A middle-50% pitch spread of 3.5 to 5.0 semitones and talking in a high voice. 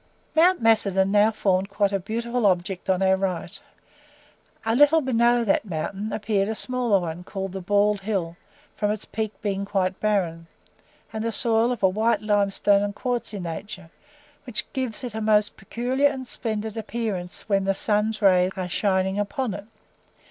No: average, 2.8 semitones; high, 205 Hz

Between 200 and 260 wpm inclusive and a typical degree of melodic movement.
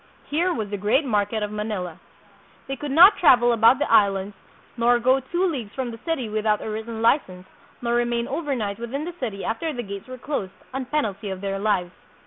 Yes: fast, 205 wpm; average, 4.5 semitones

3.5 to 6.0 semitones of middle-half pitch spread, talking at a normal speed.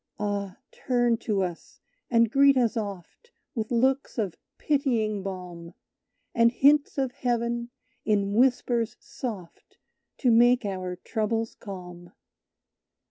No: average, 3.8 semitones; slow, 115 wpm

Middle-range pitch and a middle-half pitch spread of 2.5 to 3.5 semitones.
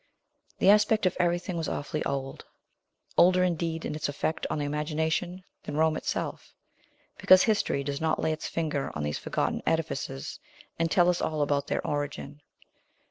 Yes: medium, 160 Hz; average, 3.2 semitones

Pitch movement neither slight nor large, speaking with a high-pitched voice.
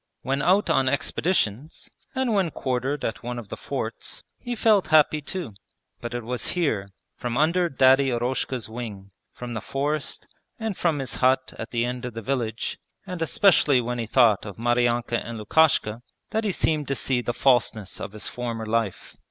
No: average, 4.7 semitones; low, 125 Hz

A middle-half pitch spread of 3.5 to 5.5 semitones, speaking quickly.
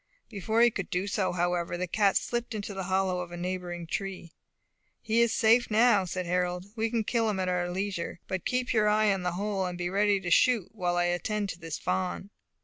No: average, 3.1 semitones; fast, 225 wpm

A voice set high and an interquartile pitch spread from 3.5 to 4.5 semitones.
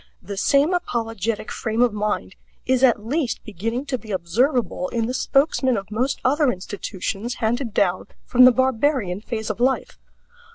Yes: high, 230 Hz; average, 3.9 semitones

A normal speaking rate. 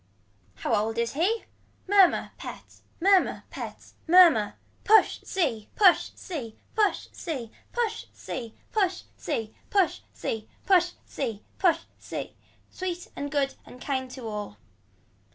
No: slow, 125 wpm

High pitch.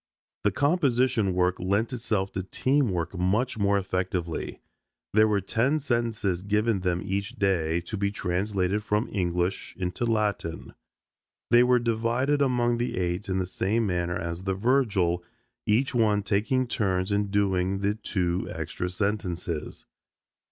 No: low, 100 Hz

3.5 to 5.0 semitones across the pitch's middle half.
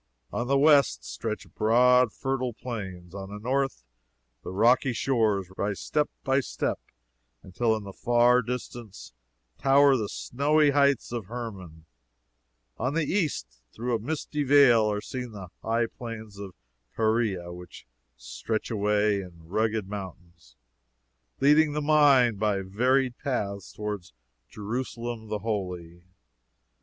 Yes: average, 4.5 semitones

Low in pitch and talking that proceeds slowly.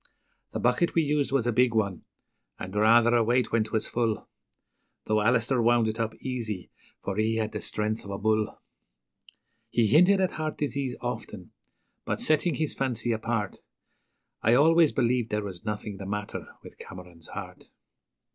No: low, 115 Hz; average, 165 wpm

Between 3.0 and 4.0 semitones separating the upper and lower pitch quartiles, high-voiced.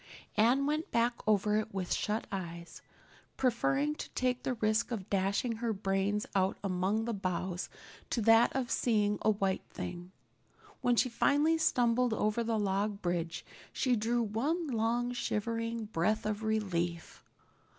Yes: average, 3.4 semitones; high, 220 Hz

